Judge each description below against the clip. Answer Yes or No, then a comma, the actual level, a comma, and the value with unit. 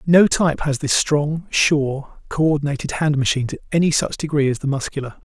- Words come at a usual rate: Yes, average, 180 wpm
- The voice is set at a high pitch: No, medium, 145 Hz